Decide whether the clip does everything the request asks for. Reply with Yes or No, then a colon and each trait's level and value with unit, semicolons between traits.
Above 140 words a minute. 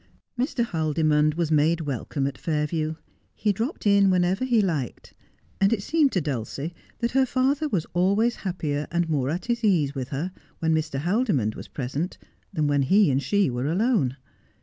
Yes: average, 175 wpm